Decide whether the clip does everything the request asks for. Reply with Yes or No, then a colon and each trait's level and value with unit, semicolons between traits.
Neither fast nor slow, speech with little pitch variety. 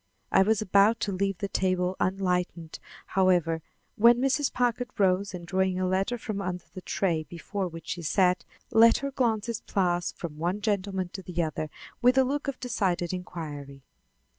No: average, 170 wpm; average, 3.4 semitones